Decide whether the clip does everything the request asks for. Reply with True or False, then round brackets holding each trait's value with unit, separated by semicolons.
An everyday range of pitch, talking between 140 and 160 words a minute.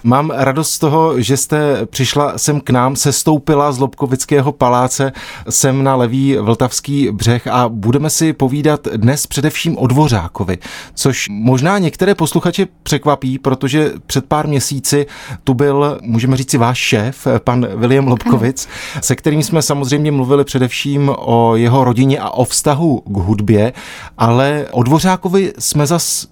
True (3.0 semitones; 145 wpm)